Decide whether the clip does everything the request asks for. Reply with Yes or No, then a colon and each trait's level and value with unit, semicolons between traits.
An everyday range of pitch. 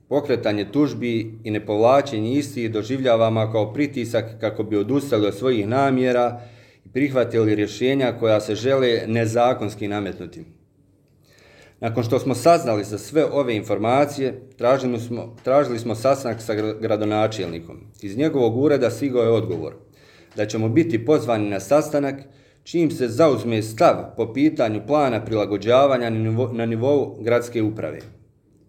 Yes: average, 3.7 semitones